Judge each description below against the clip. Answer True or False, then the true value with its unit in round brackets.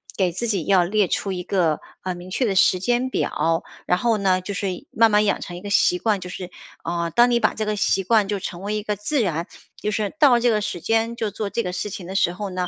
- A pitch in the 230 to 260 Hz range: False (200 Hz)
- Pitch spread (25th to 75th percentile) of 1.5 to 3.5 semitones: True (3.1 semitones)